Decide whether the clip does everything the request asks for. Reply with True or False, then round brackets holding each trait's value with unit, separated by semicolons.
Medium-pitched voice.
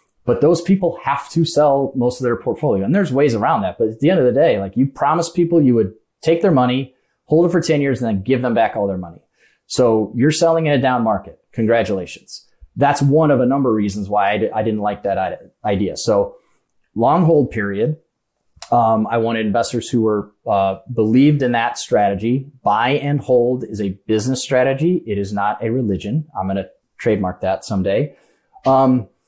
False (125 Hz)